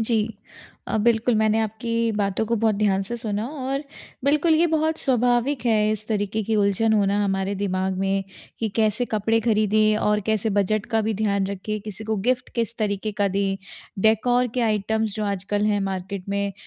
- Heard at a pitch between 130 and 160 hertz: No, high, 215 Hz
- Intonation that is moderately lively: No, narrow, 2.2 semitones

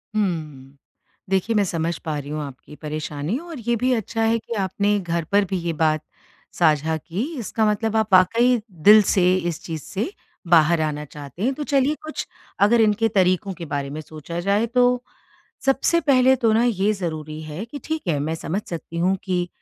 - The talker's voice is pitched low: No, medium, 185 Hz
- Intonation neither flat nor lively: No, wide, 6.2 semitones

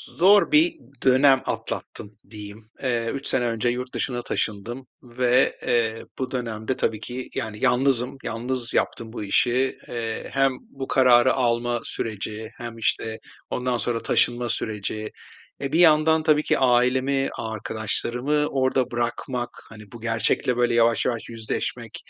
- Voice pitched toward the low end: Yes, low, 120 Hz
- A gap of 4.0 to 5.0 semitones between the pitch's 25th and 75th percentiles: No, narrow, 2.6 semitones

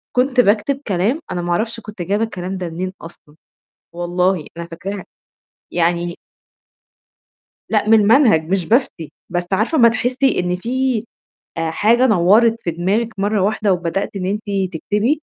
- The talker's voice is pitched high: Yes, high, 200 Hz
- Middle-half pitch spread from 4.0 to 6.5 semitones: Yes, average, 4.5 semitones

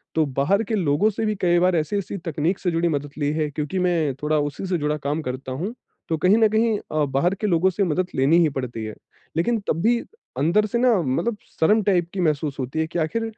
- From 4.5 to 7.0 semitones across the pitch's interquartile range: Yes, average, 5.2 semitones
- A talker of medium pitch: Yes, medium, 165 Hz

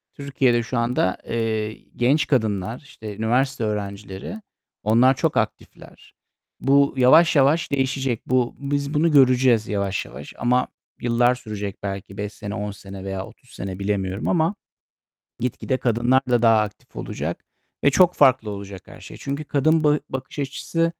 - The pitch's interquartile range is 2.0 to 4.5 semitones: No, average, 5.0 semitones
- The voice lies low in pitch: Yes, low, 120 Hz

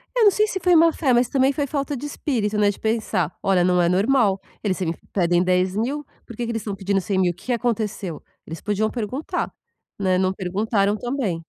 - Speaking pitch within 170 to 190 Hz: No, high, 210 Hz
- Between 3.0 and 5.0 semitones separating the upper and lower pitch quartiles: No, wide, 5.4 semitones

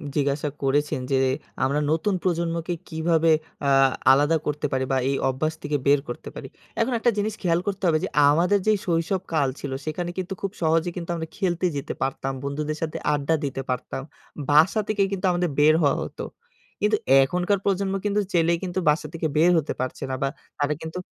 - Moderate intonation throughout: Yes, average, 3.7 semitones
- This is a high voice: No, medium, 160 Hz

